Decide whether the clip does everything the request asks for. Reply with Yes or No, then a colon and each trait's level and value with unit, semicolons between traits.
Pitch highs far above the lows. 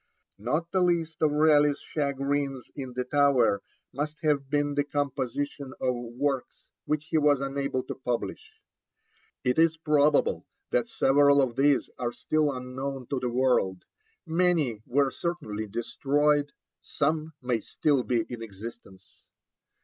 No: average, 2.9 semitones